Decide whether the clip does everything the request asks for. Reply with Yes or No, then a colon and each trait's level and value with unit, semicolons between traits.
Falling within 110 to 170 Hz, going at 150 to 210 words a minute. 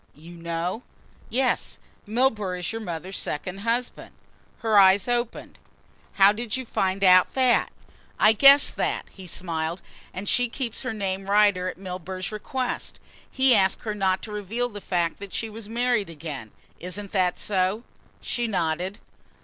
No: high, 200 Hz; average, 155 wpm